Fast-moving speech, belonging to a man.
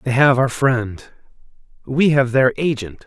No: average, 155 wpm; male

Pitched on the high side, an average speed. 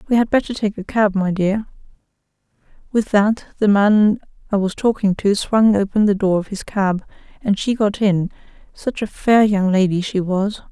Yes: high, 205 Hz; average, 185 wpm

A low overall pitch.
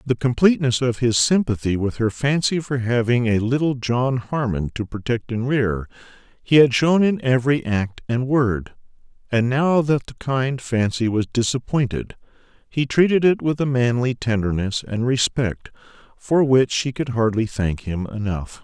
Yes: low, 125 Hz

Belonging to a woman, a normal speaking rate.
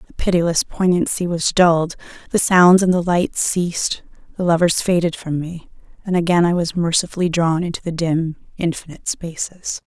Yes: female; average, 165 wpm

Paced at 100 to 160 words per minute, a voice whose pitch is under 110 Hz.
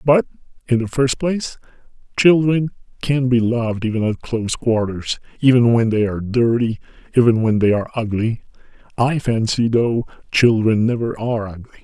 No: average, 150 wpm; low, 120 Hz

